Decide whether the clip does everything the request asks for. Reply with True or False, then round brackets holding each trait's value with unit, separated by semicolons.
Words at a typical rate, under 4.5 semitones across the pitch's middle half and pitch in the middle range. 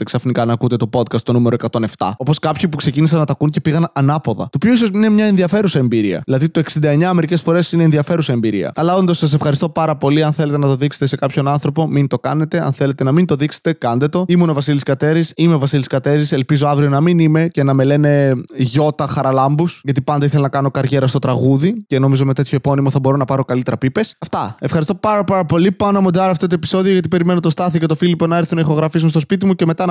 False (245 wpm; 3.6 semitones; 150 Hz)